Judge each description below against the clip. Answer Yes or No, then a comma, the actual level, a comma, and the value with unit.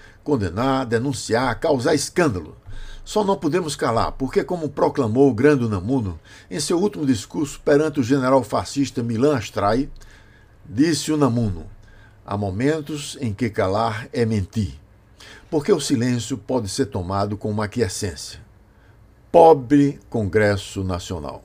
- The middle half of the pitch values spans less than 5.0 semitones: No, wide, 5.4 semitones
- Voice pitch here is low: Yes, low, 115 Hz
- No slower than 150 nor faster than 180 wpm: No, average, 125 wpm